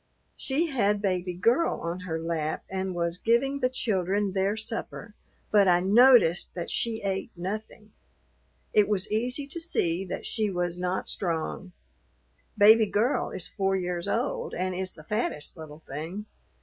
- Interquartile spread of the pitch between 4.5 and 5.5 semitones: No, average, 3.9 semitones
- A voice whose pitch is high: Yes, high, 195 Hz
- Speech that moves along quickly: No, average, 155 wpm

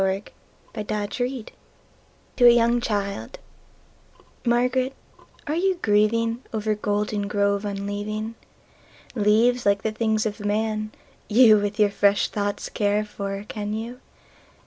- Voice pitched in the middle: No, high, 215 Hz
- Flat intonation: Yes, narrow, 2.1 semitones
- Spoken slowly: Yes, slow, 100 wpm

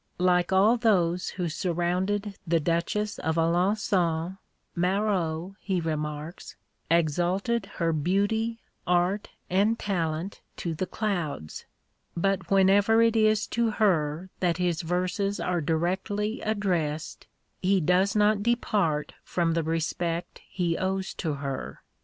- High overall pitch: No, medium, 180 Hz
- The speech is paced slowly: Yes, slow, 120 wpm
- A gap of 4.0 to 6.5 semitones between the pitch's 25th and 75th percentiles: No, average, 3.5 semitones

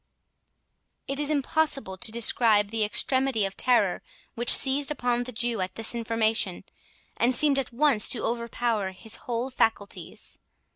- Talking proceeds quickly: No, average, 145 wpm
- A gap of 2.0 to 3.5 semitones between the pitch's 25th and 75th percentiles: Yes, average, 3.2 semitones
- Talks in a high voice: Yes, high, 235 Hz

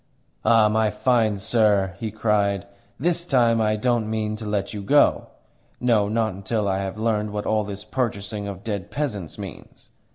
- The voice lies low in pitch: Yes, low, 105 Hz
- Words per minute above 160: Yes, average, 170 wpm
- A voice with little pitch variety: Yes, narrow, 2.2 semitones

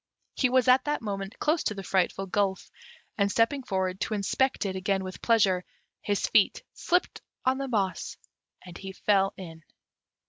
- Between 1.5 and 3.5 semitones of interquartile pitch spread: No, average, 4.8 semitones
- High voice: Yes, high, 200 Hz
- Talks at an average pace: Yes, average, 170 wpm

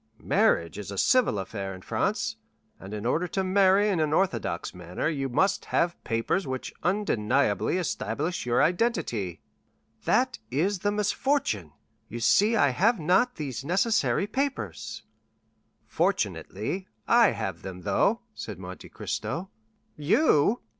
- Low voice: No, medium, 155 Hz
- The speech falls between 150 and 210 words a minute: No, slow, 135 wpm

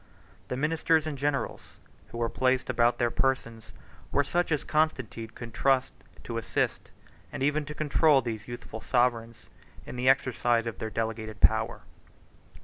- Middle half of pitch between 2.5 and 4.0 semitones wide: Yes, average, 3.7 semitones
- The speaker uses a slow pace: No, average, 150 wpm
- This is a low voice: Yes, low, 125 Hz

